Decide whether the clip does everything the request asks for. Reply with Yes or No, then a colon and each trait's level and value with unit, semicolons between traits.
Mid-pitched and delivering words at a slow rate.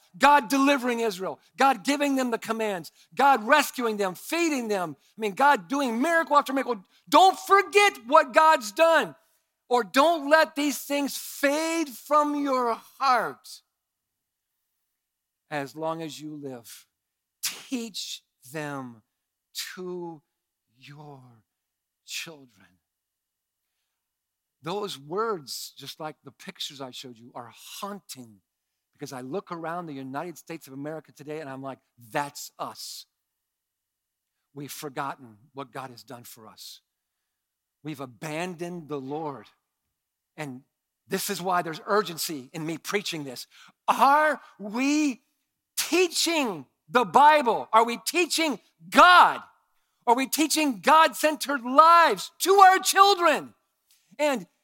No: high, 195 Hz; slow, 120 wpm